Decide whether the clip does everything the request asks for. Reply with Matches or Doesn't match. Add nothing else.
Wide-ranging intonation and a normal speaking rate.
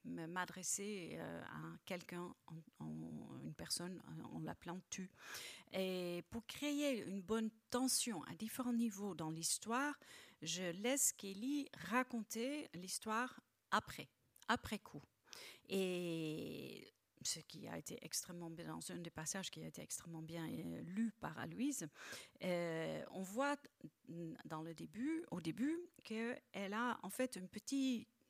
Doesn't match